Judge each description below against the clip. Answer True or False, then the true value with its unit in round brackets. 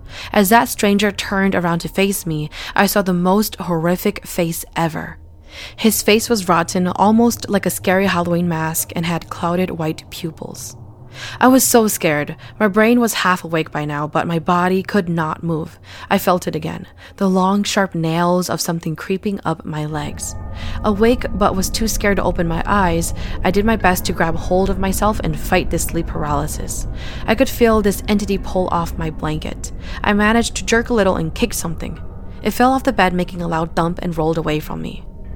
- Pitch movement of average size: True (4.2 semitones)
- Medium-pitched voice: True (180 Hz)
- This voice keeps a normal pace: True (195 wpm)